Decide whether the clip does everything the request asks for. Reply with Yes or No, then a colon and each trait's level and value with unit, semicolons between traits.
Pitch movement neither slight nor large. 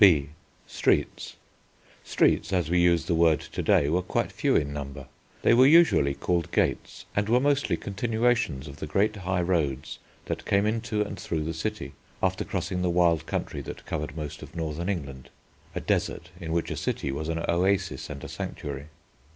Yes: average, 4.9 semitones